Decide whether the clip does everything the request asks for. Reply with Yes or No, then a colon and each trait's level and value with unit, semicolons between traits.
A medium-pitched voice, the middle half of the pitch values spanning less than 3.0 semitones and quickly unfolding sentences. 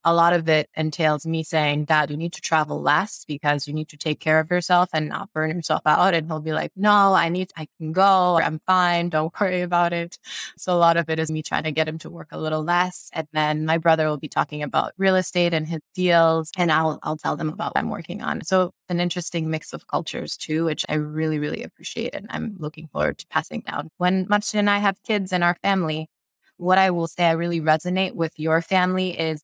Yes: medium, 165 Hz; narrow, 2.4 semitones; fast, 245 wpm